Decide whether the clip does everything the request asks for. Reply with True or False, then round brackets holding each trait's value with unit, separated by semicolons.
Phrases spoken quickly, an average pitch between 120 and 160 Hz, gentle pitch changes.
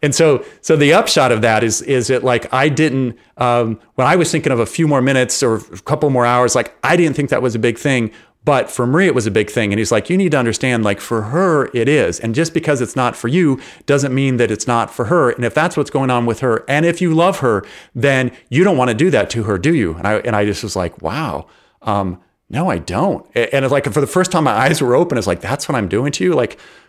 False (285 wpm; 125 Hz; 4.4 semitones)